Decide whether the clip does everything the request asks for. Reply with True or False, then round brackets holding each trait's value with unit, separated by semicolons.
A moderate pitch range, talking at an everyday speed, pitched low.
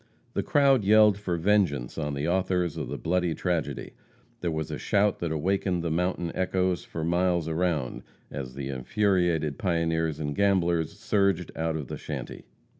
True (3.1 semitones; 165 wpm; 85 Hz)